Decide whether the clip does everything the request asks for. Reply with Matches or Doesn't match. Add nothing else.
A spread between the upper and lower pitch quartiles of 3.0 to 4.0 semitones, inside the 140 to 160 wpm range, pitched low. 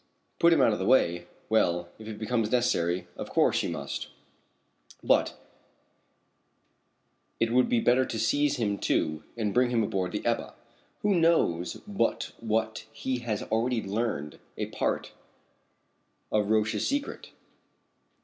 Matches